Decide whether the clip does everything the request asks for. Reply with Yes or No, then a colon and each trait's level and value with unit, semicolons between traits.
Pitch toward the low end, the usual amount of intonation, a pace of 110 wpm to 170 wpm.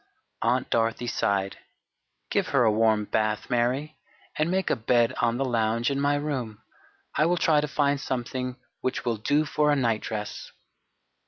Yes: low, 125 Hz; average, 4.2 semitones; average, 165 wpm